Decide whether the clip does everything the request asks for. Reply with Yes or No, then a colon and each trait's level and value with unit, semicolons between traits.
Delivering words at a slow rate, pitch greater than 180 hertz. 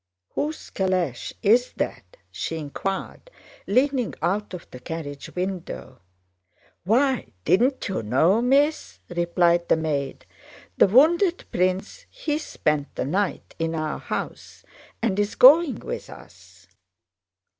Yes: slow, 120 wpm; high, 190 Hz